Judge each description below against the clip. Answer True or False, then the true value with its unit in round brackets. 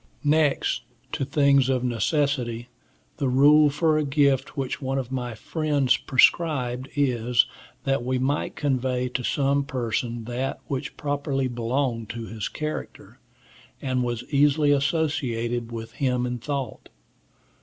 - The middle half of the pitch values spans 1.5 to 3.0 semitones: True (2.7 semitones)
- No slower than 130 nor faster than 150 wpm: True (135 wpm)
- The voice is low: True (130 Hz)